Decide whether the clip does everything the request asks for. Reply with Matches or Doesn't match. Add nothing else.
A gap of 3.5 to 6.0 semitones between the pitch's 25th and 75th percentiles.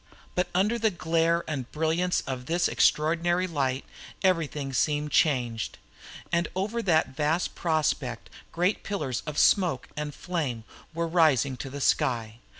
Matches